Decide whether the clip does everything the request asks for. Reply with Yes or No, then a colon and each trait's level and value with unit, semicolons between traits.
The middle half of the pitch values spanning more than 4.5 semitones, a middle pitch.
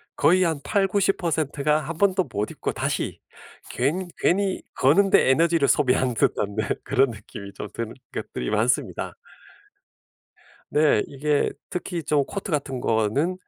Yes: wide, 5.5 semitones; medium, 150 Hz